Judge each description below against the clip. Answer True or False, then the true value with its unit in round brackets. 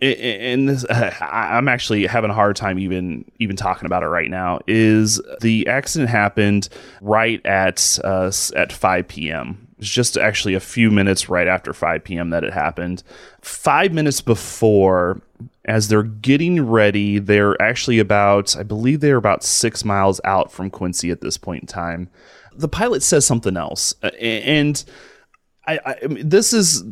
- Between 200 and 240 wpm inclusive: False (165 wpm)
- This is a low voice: True (105 Hz)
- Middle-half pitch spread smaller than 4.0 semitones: False (4.3 semitones)